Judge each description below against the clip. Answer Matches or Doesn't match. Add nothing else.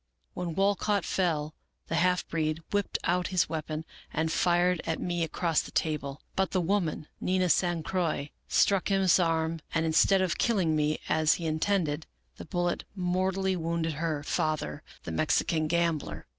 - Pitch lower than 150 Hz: Doesn't match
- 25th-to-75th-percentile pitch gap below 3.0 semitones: Matches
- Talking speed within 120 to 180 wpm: Matches